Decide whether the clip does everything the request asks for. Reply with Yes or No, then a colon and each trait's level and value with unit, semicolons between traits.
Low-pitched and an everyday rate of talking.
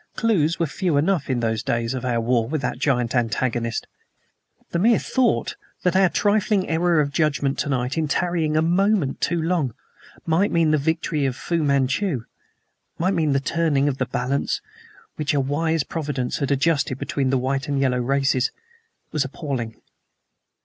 No: medium, 145 Hz; average, 170 wpm